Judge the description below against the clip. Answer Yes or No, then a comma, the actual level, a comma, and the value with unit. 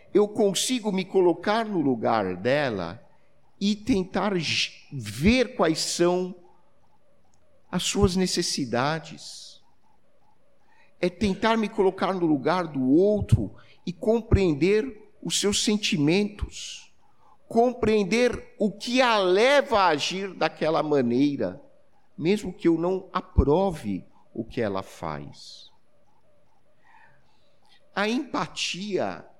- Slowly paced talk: Yes, slow, 100 wpm